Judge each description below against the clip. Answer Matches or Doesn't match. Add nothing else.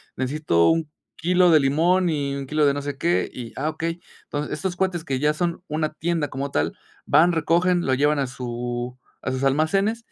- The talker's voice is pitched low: Doesn't match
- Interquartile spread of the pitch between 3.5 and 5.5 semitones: Matches